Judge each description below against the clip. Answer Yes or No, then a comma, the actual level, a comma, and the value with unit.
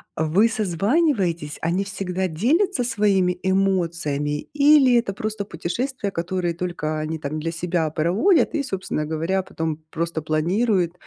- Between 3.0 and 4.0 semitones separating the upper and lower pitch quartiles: No, average, 4.7 semitones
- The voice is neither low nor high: Yes, medium, 180 Hz